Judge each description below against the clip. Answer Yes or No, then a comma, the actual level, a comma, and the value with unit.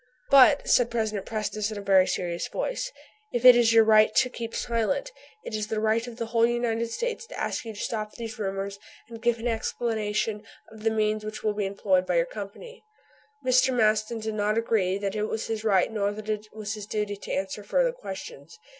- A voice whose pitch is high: Yes, high, 220 Hz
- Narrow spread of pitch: Yes, narrow, 2.0 semitones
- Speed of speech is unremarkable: No, fast, 215 wpm